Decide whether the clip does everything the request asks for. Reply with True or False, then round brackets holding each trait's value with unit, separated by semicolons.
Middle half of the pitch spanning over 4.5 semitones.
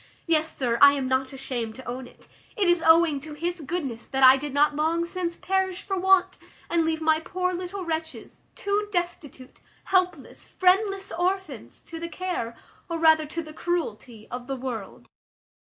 True (5.1 semitones)